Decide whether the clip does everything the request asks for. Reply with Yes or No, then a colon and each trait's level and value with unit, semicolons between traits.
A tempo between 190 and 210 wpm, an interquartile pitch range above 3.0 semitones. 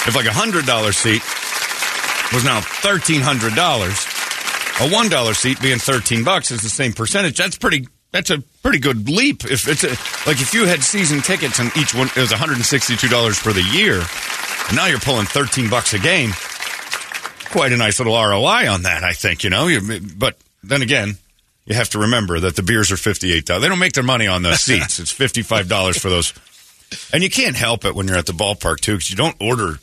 Yes: average, 200 wpm; average, 5.1 semitones